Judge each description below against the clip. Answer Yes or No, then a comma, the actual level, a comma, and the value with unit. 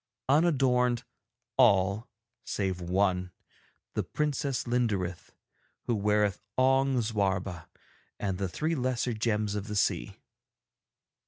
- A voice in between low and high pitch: No, low, 110 Hz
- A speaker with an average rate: No, slow, 100 wpm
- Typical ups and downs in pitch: Yes, average, 4.7 semitones